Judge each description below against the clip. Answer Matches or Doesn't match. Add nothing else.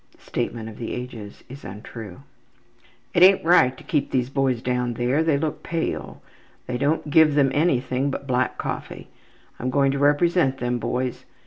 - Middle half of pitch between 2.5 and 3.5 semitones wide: Matches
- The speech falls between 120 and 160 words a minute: Doesn't match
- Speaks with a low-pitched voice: Matches